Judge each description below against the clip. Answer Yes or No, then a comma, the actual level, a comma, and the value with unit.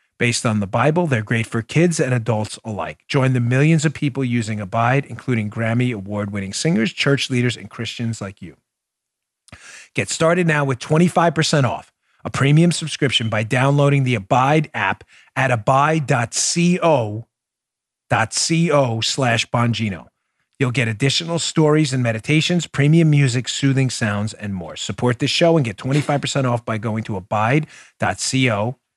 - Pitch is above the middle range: No, low, 130 Hz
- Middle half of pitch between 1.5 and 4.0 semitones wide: No, average, 4.6 semitones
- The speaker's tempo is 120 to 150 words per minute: Yes, average, 145 wpm